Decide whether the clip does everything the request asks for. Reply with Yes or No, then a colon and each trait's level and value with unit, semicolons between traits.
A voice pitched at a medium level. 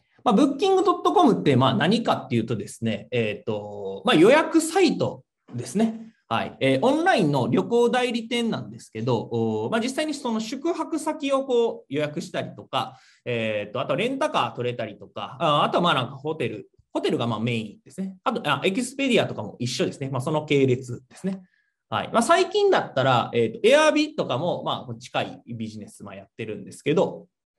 Yes: medium, 175 Hz